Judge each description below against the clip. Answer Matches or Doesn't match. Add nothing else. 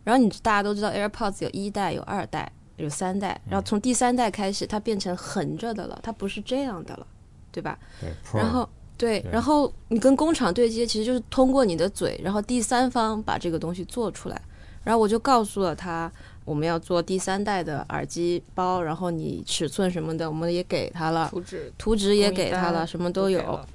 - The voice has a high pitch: Matches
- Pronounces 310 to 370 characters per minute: Matches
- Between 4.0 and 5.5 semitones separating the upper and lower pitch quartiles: Matches